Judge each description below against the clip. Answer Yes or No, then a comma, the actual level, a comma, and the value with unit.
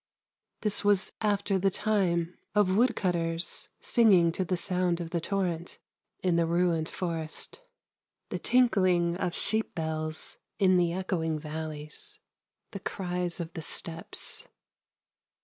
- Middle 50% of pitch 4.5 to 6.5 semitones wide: No, average, 2.9 semitones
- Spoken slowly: Yes, slow, 125 wpm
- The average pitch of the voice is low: No, medium, 180 Hz